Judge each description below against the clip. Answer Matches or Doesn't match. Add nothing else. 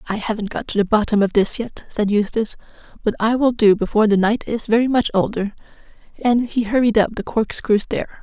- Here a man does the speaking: Doesn't match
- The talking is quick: Matches